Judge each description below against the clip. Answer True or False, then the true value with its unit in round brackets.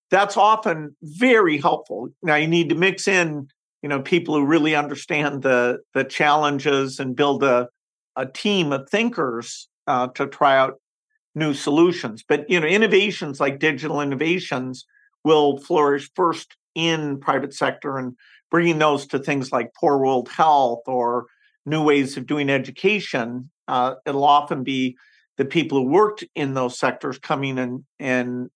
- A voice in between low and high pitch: True (145 Hz)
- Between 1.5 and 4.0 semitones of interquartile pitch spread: True (3.7 semitones)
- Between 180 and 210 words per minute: False (160 wpm)